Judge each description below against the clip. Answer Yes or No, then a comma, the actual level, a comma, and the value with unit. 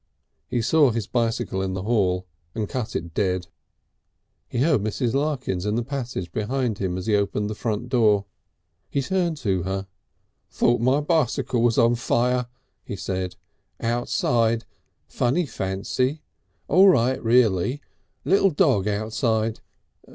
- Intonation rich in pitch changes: No, average, 4.2 semitones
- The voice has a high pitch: No, low, 115 Hz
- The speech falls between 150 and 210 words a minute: No, average, 140 wpm